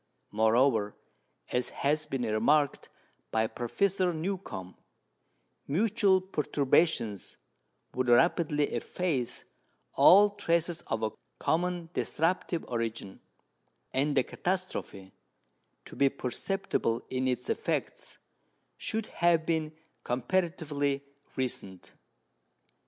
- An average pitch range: No, wide, 6.3 semitones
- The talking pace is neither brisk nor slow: No, slow, 90 wpm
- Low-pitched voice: No, medium, 145 Hz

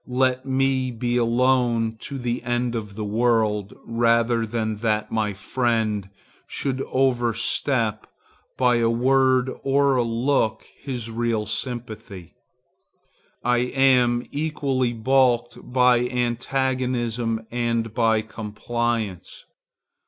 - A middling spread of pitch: No, narrow, 2.1 semitones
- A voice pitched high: No, low, 120 Hz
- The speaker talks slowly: Yes, slow, 105 wpm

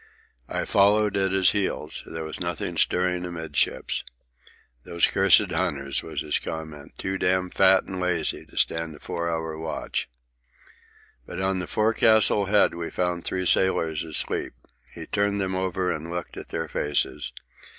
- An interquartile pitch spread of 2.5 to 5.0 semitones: Yes, average, 2.9 semitones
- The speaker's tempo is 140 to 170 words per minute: Yes, average, 155 wpm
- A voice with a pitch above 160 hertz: No, very low, 90 Hz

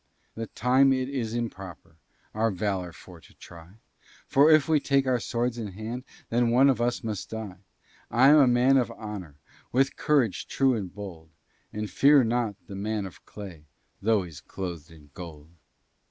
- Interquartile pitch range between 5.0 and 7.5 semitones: Yes, average, 5.3 semitones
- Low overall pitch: Yes, low, 110 Hz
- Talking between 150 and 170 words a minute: No, average, 180 wpm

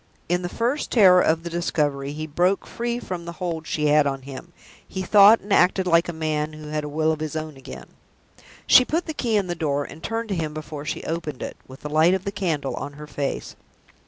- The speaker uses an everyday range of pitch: Yes, average, 3.8 semitones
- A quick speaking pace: Yes, fast, 240 wpm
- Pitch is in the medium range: Yes, medium, 160 Hz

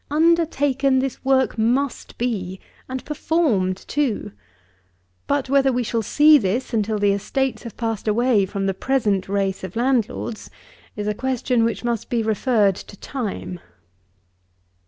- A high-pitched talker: Yes, high, 235 Hz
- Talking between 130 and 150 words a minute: Yes, average, 140 wpm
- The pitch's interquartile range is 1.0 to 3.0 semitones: No, average, 4.6 semitones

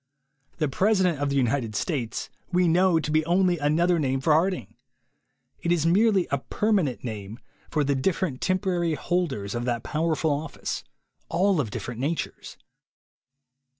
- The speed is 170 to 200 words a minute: No, average, 150 wpm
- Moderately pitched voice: Yes, medium, 160 Hz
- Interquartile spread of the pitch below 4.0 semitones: No, average, 5.0 semitones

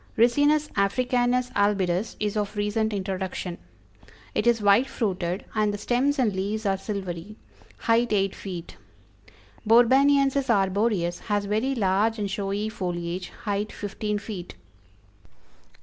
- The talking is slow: Yes, slow, 120 wpm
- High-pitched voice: Yes, high, 210 Hz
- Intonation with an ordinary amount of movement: Yes, average, 3.2 semitones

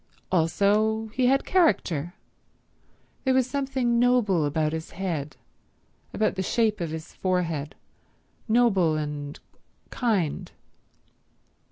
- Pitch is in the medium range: No, high, 195 Hz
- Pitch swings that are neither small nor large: No, wide, 6.9 semitones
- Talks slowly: Yes, slow, 95 wpm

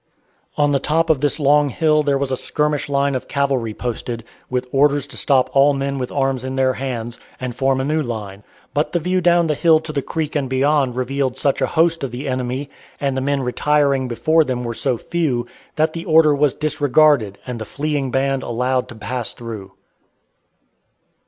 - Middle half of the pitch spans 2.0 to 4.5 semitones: Yes, average, 2.8 semitones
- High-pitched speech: No, low, 135 Hz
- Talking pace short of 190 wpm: No, average, 200 wpm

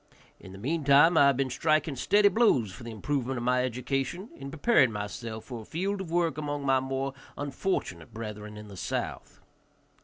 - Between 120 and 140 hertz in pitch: Yes, low, 135 Hz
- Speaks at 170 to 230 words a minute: Yes, average, 185 wpm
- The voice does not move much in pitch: No, average, 5.0 semitones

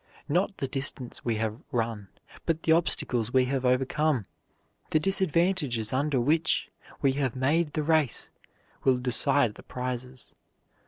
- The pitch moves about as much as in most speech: Yes, average, 3.9 semitones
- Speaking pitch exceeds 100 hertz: Yes, low, 135 Hz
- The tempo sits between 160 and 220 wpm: No, average, 140 wpm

